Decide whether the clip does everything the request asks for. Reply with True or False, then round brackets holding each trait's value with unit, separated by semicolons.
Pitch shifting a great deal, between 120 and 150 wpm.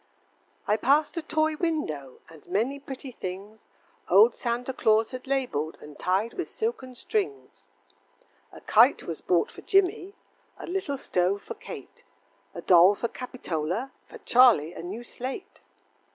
True (8.4 semitones; 145 wpm)